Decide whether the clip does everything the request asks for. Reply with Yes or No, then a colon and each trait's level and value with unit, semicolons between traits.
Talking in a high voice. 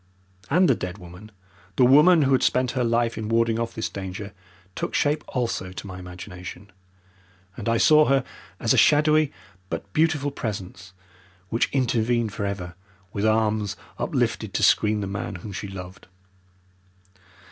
No: low, 110 Hz